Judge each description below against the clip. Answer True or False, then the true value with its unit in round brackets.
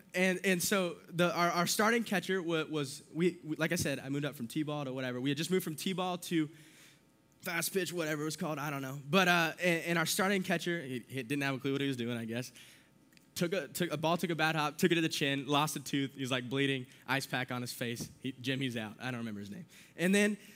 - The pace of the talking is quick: True (275 wpm)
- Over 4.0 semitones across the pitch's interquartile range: True (4.6 semitones)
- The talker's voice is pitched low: False (155 Hz)